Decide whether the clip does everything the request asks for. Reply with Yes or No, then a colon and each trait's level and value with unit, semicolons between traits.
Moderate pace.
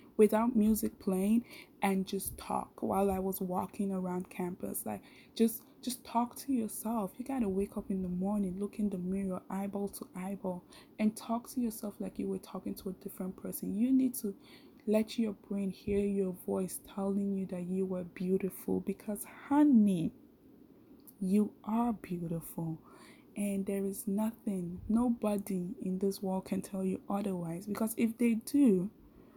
Yes: average, 165 wpm